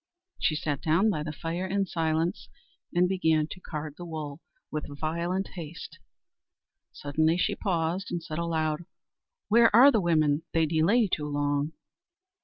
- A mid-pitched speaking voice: Yes, medium, 165 Hz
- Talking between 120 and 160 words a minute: Yes, average, 150 wpm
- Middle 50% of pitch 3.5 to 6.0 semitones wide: No, average, 2.8 semitones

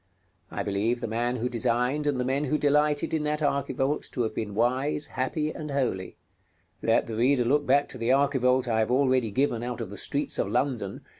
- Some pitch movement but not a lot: Yes, average, 3.3 semitones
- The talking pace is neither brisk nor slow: No, fast, 225 wpm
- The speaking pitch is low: Yes, low, 130 Hz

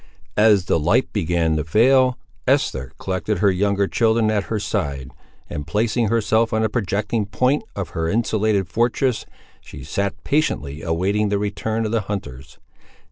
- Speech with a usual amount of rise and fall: Yes, average, 4.2 semitones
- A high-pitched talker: No, low, 105 Hz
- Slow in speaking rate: No, average, 155 wpm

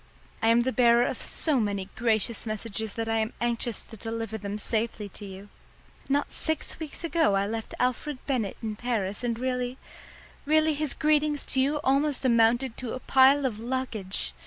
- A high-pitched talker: Yes, high, 235 Hz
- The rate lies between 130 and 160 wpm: No, average, 180 wpm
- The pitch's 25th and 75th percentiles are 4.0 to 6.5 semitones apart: No, average, 3.4 semitones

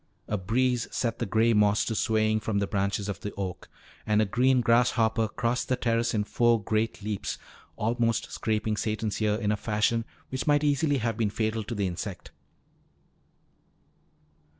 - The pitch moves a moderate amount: No, narrow, 2.1 semitones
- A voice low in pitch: Yes, low, 110 Hz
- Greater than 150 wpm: Yes, average, 170 wpm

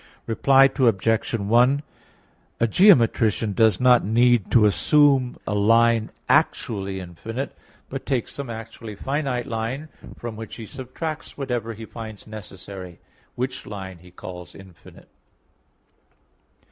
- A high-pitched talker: No, low, 115 Hz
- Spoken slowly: Yes, slow, 120 wpm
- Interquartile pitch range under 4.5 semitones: Yes, average, 3.7 semitones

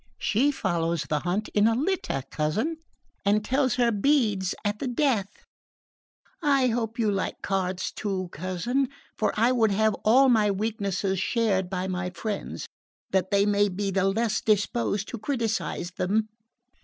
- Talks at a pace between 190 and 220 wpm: No, average, 155 wpm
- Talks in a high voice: Yes, high, 210 Hz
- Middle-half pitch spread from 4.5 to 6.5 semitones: No, average, 3.7 semitones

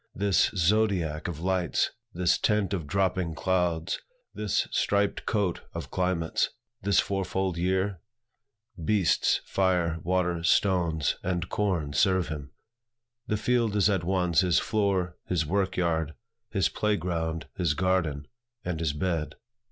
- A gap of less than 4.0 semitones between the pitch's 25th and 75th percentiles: Yes, average, 2.8 semitones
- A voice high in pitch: No, very low, 90 Hz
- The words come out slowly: Yes, slow, 130 wpm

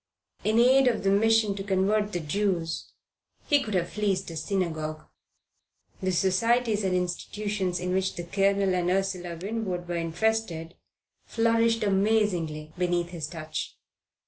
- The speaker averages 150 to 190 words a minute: No, average, 140 wpm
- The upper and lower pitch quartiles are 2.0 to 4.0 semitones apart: Yes, average, 3.5 semitones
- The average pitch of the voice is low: No, high, 190 Hz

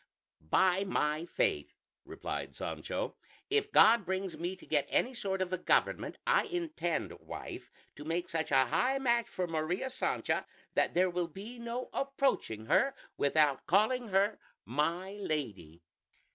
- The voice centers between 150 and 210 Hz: Yes, medium, 185 Hz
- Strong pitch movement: Yes, wide, 7.2 semitones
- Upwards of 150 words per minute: No, average, 145 wpm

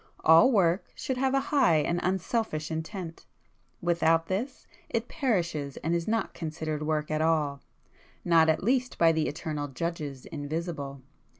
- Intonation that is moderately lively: Yes, average, 3.8 semitones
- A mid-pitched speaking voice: Yes, medium, 165 Hz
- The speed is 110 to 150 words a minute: Yes, slow, 135 wpm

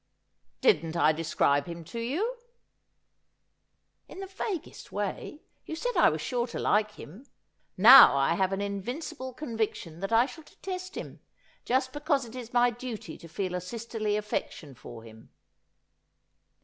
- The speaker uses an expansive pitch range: Yes, wide, 6.5 semitones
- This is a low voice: No, high, 225 Hz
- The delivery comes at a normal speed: Yes, average, 160 wpm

